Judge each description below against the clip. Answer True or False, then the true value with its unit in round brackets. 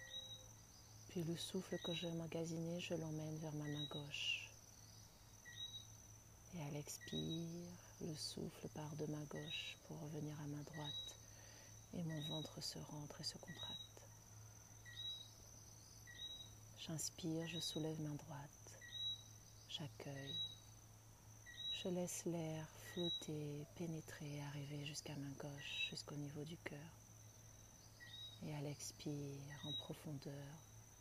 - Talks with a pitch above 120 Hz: True (135 Hz)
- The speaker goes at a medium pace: False (120 wpm)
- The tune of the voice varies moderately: False (5.9 semitones)